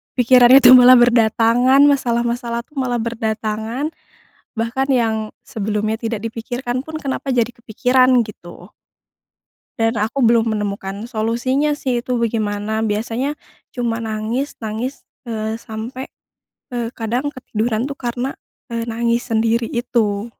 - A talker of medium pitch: No, high, 235 Hz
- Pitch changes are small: Yes, narrow, 2.3 semitones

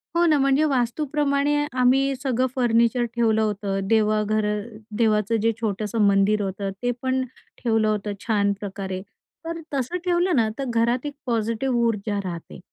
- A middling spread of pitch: Yes, average, 4.0 semitones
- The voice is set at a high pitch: Yes, high, 230 Hz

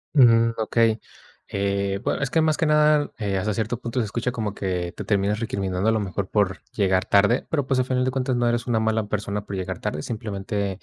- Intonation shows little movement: No, average, 3.5 semitones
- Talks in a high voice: No, low, 110 Hz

